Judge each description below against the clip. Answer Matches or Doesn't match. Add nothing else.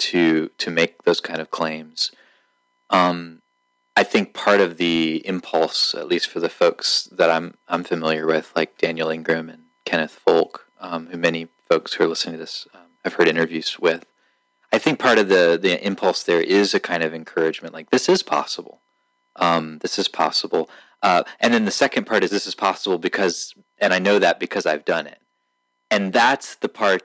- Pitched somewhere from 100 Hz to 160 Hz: Doesn't match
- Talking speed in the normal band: Matches